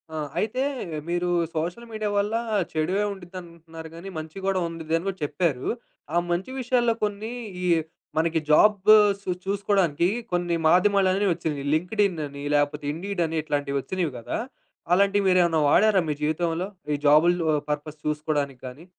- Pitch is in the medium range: Yes, medium, 175 Hz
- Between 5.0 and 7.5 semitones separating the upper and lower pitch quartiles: No, average, 4.0 semitones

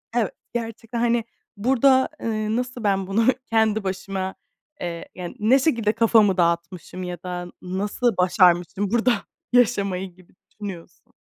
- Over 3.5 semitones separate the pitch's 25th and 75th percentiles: Yes, average, 4.0 semitones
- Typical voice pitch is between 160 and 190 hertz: No, high, 205 Hz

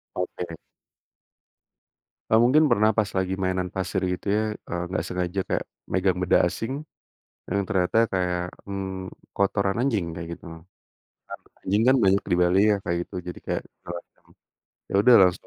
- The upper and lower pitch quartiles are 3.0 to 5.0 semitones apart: No, narrow, 2.4 semitones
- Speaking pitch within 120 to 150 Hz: No, very low, 95 Hz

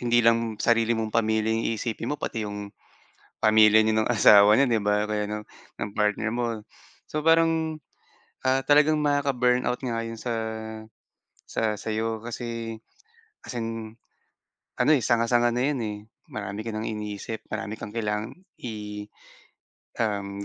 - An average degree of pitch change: No, narrow, 2.2 semitones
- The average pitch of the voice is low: Yes, low, 115 Hz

